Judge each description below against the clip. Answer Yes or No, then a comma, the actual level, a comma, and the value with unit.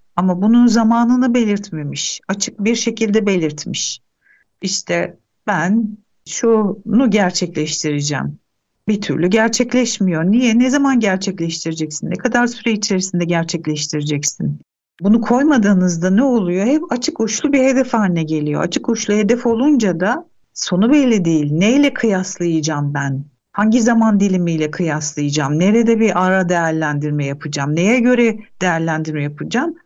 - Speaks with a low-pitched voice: No, high, 195 Hz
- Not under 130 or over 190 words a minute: No, average, 120 wpm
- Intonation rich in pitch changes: Yes, wide, 6.5 semitones